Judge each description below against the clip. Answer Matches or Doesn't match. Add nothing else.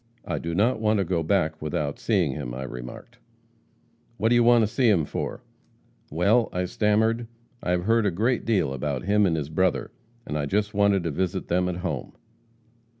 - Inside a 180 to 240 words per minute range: Matches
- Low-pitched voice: Matches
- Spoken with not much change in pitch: Doesn't match